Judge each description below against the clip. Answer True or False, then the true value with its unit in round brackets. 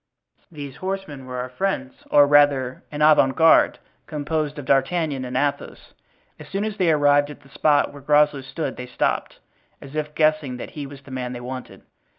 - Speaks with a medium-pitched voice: True (145 Hz)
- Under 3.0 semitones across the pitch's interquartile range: True (2.5 semitones)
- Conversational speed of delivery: True (185 wpm)